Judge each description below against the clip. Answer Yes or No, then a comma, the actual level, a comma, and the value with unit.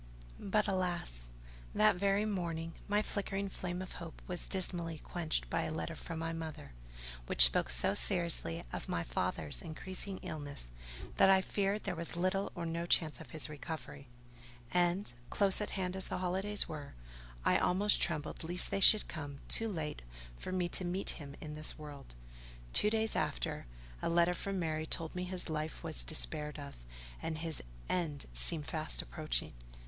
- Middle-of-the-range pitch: Yes, medium, 170 Hz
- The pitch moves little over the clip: No, average, 3.5 semitones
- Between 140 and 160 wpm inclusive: No, average, 170 wpm